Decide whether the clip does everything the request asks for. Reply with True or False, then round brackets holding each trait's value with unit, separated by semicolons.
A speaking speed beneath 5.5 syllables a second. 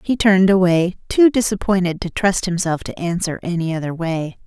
True (5.3 syllables/s)